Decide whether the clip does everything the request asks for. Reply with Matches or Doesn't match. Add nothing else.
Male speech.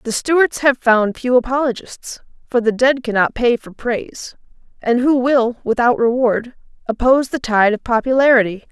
Doesn't match